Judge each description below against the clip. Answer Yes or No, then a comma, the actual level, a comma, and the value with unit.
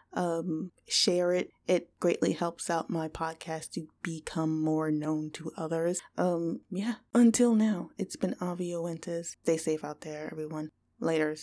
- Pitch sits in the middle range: Yes, medium, 165 Hz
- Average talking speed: Yes, average, 145 wpm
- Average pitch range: No, narrow, 2.1 semitones